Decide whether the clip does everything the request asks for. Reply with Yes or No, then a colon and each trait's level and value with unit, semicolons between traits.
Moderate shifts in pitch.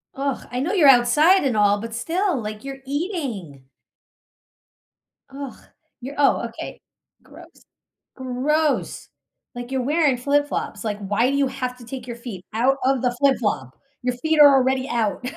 Yes: average, 3.2 semitones